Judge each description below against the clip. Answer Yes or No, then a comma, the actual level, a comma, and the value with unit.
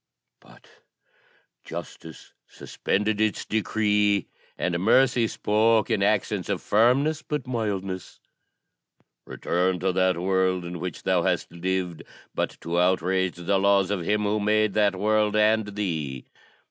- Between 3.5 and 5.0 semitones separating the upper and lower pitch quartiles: No, average, 2.7 semitones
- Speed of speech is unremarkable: No, slow, 130 wpm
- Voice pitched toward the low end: Yes, low, 100 Hz